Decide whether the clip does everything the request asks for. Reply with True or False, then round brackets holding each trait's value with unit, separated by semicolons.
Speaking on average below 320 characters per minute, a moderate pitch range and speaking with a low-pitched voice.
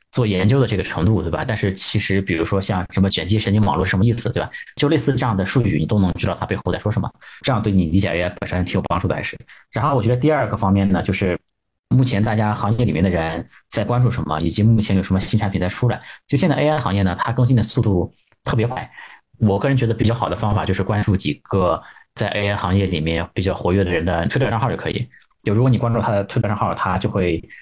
False (390 characters per minute; 3.4 semitones; 100 Hz)